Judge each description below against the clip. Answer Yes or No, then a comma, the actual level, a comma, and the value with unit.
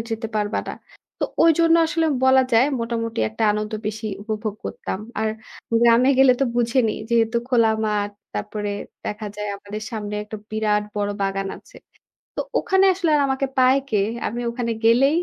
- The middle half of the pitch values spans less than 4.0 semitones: Yes, average, 3.5 semitones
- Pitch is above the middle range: Yes, high, 225 Hz